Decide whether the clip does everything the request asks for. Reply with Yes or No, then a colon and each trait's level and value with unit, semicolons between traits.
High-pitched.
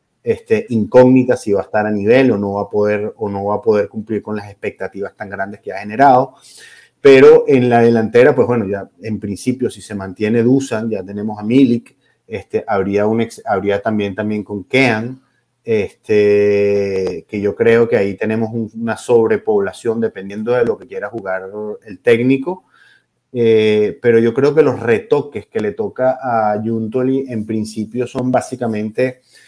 No: low, 110 Hz